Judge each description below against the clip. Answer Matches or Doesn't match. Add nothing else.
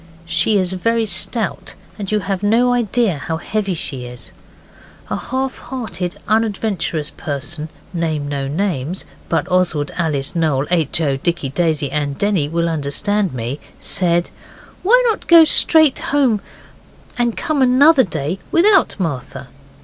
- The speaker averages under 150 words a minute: Matches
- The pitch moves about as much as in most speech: Doesn't match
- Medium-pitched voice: Matches